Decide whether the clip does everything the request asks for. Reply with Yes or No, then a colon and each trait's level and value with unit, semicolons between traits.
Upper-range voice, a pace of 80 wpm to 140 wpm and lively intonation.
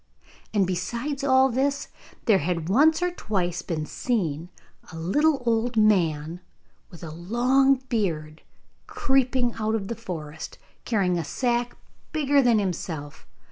Yes: high, 215 Hz; slow, 135 wpm; wide, 7.1 semitones